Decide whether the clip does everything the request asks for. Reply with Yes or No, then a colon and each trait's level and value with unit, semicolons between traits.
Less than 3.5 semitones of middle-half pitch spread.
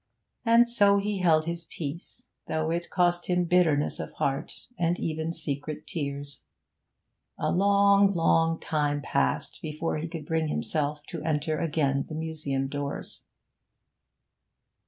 Yes: average, 2.9 semitones